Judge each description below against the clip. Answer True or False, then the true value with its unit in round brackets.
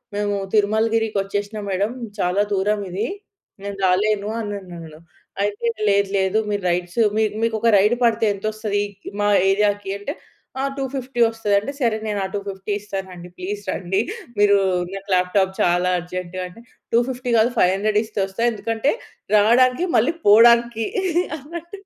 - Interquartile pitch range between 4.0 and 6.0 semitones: False (2.8 semitones)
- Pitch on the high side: True (205 Hz)